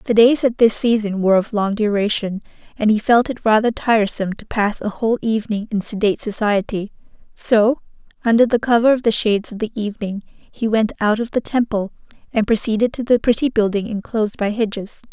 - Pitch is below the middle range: No, high, 220 Hz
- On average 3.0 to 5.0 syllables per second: No, 5.8 syllables/s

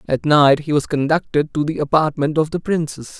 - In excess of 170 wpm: Yes, fast, 205 wpm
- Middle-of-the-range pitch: Yes, medium, 150 Hz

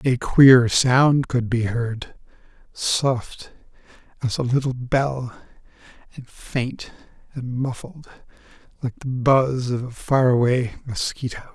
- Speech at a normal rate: No, slow, 120 wpm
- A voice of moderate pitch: No, low, 125 Hz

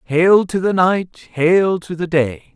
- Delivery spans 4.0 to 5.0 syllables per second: No, 3.5 syllables/s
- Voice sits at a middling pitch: Yes, medium, 170 Hz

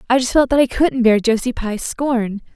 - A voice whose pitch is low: No, high, 245 Hz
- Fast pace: Yes, fast, 235 wpm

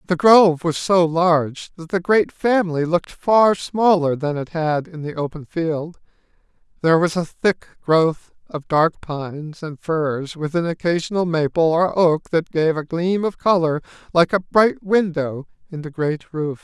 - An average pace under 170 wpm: No, average, 175 wpm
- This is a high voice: No, medium, 165 Hz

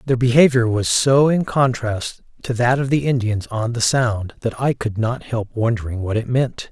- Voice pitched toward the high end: No, low, 120 Hz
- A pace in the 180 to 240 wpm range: Yes, fast, 205 wpm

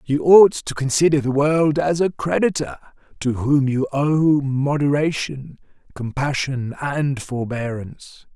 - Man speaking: Yes, male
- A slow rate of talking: Yes, slow, 120 wpm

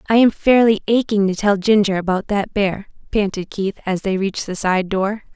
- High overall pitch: Yes, high, 200 Hz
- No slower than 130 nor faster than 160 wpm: No, average, 200 wpm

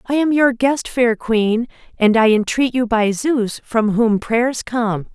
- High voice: Yes, high, 235 Hz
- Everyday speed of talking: Yes, average, 185 wpm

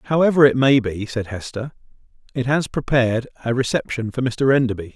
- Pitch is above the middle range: No, low, 125 Hz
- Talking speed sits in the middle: Yes, average, 170 wpm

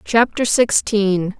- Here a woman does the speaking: Yes, female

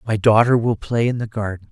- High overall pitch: No, low, 110 Hz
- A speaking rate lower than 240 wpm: No, fast, 245 wpm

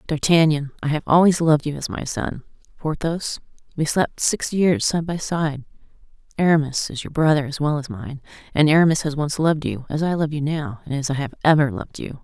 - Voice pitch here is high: No, medium, 150 Hz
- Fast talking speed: Yes, fast, 210 wpm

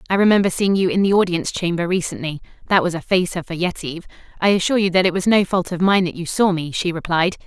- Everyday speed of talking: No, fast, 250 wpm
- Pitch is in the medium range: Yes, medium, 180 Hz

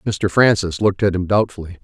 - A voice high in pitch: No, very low, 95 Hz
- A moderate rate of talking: Yes, average, 195 wpm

